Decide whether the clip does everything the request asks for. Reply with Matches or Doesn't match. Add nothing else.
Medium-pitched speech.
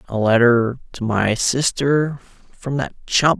Doesn't match